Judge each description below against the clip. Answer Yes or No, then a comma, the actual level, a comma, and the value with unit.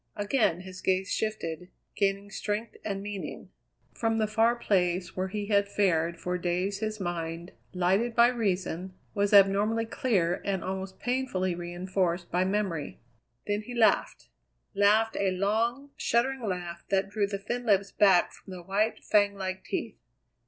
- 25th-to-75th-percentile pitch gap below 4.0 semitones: Yes, average, 2.8 semitones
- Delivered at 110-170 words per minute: Yes, average, 150 wpm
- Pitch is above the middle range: Yes, high, 200 Hz